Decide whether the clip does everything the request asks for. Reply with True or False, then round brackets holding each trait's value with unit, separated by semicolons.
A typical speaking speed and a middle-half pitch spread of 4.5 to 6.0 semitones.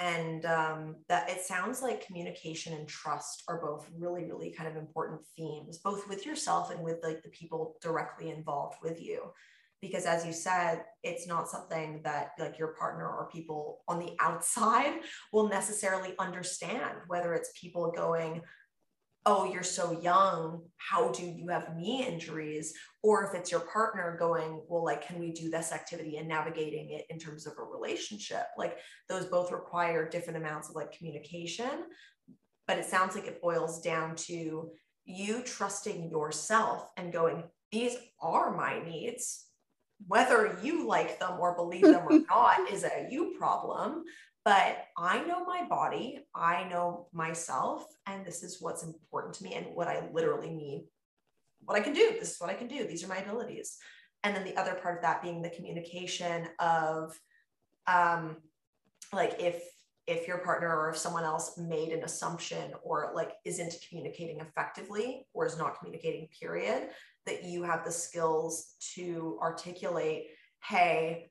False (165 wpm; 3.3 semitones)